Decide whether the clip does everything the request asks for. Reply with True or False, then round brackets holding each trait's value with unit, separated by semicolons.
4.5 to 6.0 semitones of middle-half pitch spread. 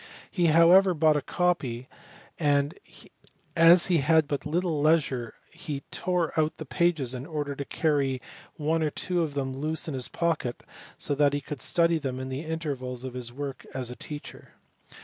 False (3.6 semitones)